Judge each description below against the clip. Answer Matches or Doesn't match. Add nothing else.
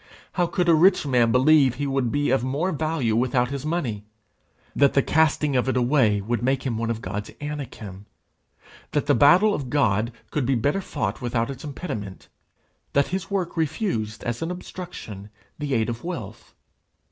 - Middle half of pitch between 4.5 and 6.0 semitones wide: Matches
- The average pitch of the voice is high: Doesn't match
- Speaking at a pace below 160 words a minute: Doesn't match